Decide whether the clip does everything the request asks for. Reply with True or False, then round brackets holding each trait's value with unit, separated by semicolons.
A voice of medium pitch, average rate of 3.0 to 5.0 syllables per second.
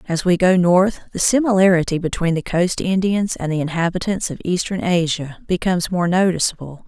False (180 Hz; 5.4 syllables/s)